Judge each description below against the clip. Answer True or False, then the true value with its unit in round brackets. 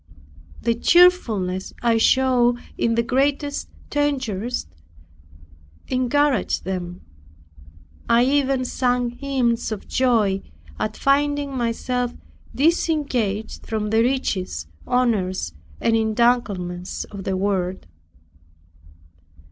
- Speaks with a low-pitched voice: False (235 Hz)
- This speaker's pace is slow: True (90 wpm)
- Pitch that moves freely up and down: False (4.3 semitones)